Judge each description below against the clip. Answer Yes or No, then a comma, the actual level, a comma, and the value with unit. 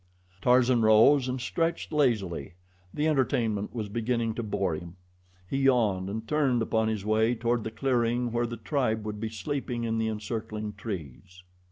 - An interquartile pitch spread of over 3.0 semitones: No, average, 2.7 semitones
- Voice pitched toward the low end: Yes, low, 115 Hz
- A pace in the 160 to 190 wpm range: Yes, average, 165 wpm